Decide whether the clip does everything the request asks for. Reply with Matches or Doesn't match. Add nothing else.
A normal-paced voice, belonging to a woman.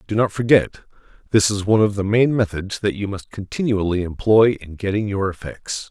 Doesn't match